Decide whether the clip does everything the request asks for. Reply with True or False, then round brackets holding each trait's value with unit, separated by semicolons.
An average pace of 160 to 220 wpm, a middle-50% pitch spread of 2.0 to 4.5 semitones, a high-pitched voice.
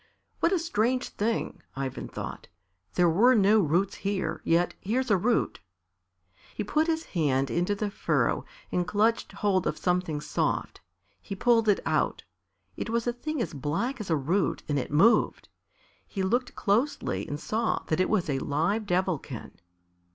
False (165 wpm; 5.3 semitones; 200 Hz)